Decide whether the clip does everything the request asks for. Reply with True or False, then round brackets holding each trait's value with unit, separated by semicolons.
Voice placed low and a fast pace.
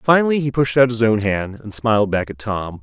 True (115 Hz; 255 wpm)